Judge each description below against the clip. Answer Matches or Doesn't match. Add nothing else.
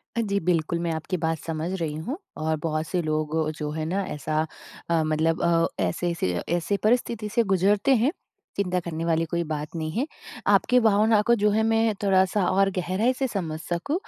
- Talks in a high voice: Doesn't match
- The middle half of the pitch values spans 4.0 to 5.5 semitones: Matches